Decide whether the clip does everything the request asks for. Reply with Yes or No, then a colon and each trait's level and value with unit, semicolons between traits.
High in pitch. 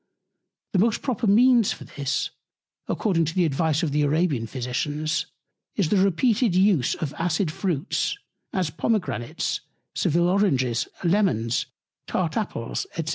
No: medium, 170 Hz